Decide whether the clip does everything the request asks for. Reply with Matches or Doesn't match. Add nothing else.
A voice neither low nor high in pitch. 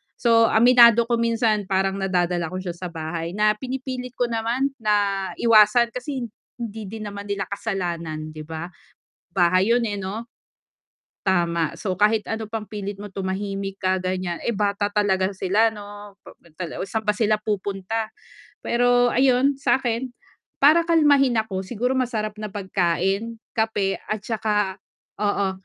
Doesn't match